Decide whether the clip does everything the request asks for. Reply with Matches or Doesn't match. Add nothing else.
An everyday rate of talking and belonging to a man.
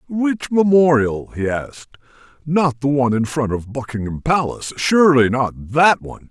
Matches